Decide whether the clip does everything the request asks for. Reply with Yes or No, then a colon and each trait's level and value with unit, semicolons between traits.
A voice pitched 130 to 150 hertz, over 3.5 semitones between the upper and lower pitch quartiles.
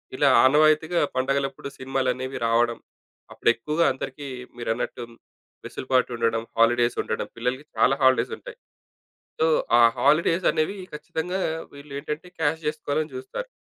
Yes: low, 135 Hz; average, 3.9 semitones